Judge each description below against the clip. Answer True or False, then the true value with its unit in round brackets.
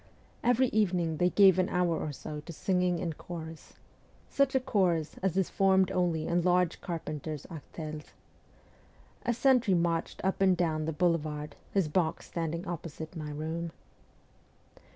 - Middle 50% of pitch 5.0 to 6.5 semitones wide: False (2.9 semitones)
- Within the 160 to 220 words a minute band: False (150 wpm)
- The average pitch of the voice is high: False (170 Hz)